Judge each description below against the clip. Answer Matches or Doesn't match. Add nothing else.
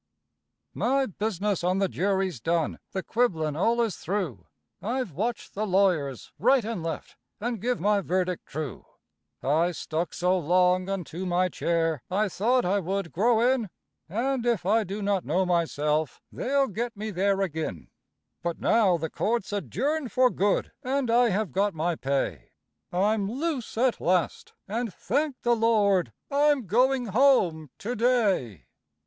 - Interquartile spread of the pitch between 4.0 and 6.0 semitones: Matches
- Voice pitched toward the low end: Doesn't match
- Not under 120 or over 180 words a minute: Matches